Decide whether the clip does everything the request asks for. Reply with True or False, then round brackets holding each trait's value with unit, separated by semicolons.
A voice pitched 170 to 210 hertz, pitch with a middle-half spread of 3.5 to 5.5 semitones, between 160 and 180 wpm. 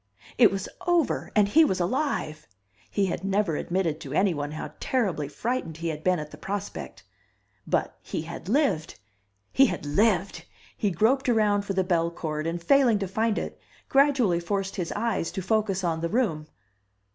True (190 Hz; 4.9 semitones; 170 wpm)